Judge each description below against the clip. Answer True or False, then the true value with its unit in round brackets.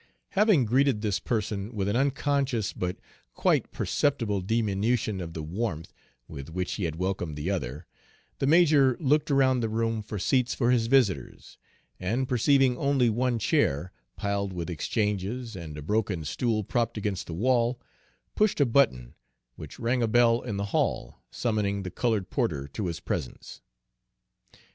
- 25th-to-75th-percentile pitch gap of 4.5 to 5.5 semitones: True (5.2 semitones)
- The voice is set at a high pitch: False (110 Hz)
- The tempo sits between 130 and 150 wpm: False (160 wpm)